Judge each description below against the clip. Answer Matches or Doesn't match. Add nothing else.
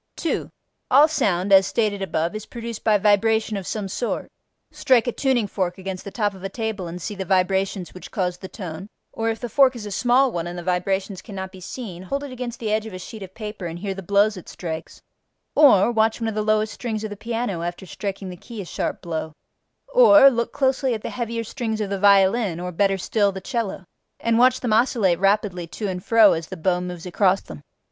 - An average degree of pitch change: Matches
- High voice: Matches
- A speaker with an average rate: Doesn't match